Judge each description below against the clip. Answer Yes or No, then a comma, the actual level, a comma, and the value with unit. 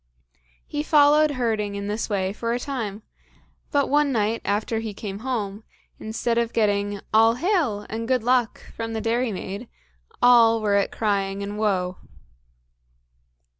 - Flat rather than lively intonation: No, average, 3.2 semitones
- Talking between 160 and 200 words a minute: No, average, 145 wpm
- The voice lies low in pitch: No, high, 225 Hz